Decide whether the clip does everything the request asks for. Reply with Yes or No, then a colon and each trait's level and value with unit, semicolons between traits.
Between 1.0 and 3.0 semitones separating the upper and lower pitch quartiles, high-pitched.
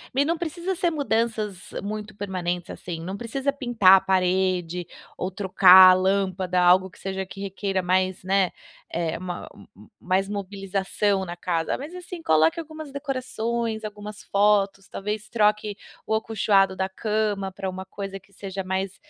Yes: narrow, 2.6 semitones; high, 195 Hz